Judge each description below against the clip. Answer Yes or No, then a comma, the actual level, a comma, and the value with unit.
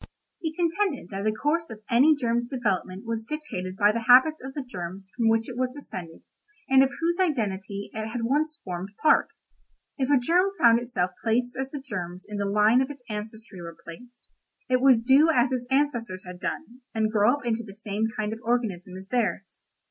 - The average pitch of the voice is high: Yes, high, 235 Hz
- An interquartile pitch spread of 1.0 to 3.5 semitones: No, average, 4.6 semitones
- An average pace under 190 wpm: No, average, 200 wpm